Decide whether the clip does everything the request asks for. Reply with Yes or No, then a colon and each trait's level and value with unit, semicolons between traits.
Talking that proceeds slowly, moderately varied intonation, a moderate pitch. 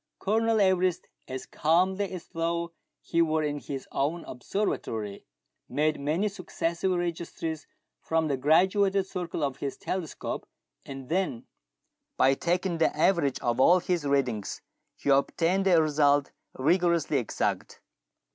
Yes: slow, 130 wpm; average, 4.4 semitones; medium, 165 Hz